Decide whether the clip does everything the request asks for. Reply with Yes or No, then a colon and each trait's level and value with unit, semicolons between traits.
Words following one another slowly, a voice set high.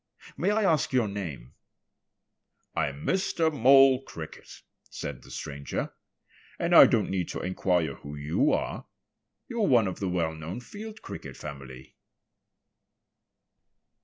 No: slow, 130 wpm; very low, 95 Hz